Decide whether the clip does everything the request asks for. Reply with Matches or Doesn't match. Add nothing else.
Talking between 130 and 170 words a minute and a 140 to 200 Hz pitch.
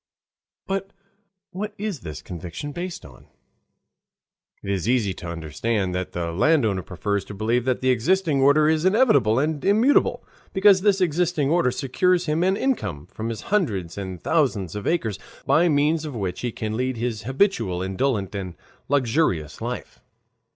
Doesn't match